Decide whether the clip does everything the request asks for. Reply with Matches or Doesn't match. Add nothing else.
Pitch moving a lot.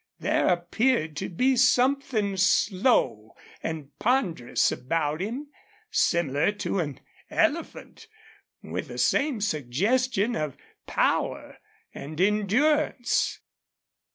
Matches